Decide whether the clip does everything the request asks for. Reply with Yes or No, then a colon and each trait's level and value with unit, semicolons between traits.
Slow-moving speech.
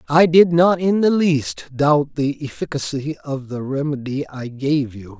No: average, 175 wpm